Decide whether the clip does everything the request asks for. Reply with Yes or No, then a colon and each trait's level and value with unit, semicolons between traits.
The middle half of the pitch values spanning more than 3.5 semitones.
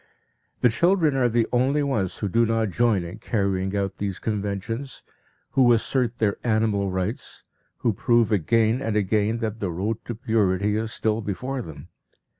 No: average, 3.0 semitones